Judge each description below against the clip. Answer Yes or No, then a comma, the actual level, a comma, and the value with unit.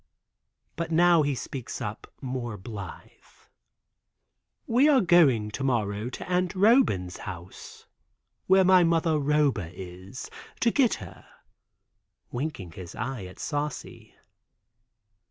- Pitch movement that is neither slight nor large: No, wide, 8.8 semitones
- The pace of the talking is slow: Yes, slow, 115 wpm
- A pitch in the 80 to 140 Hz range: Yes, low, 135 Hz